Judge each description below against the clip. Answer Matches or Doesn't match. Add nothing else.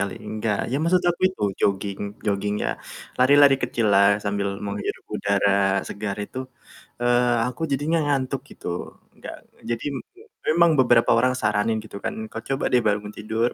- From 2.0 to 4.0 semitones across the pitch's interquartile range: Doesn't match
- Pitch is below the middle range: Matches